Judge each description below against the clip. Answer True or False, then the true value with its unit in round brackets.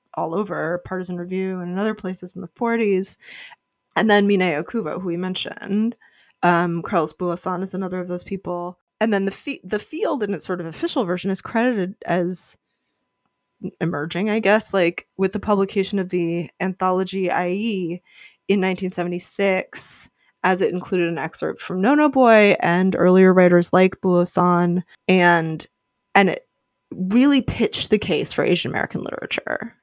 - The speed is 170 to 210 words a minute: False (160 wpm)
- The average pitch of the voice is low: False (185 Hz)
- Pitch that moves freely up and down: False (2.6 semitones)